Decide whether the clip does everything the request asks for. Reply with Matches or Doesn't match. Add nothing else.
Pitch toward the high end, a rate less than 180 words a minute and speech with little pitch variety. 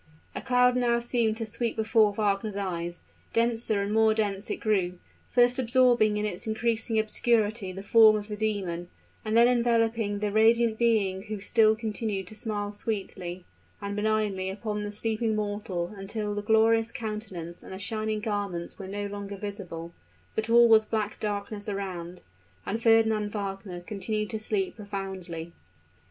Matches